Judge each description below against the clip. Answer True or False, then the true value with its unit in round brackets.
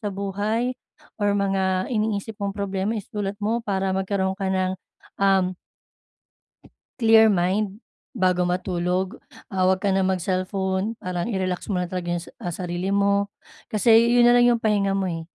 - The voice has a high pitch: True (195 Hz)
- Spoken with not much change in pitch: True (1.9 semitones)